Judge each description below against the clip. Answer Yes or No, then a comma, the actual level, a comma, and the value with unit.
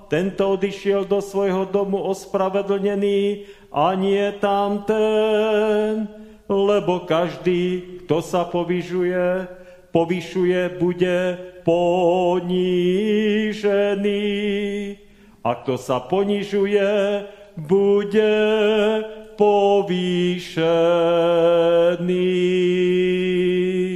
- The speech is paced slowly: Yes, slow, 60 wpm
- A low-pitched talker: No, high, 190 Hz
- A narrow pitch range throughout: Yes, narrow, 2.2 semitones